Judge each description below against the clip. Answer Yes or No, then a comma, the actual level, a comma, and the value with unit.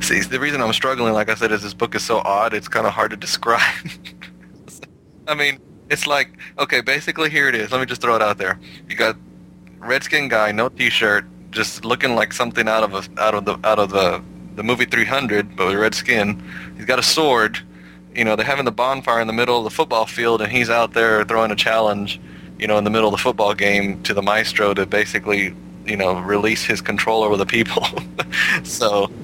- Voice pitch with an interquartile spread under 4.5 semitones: Yes, average, 2.9 semitones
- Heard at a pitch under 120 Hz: Yes, low, 105 Hz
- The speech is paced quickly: Yes, fast, 225 wpm